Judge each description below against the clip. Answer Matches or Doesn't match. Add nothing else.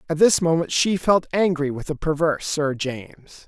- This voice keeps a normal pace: Matches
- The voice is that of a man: Matches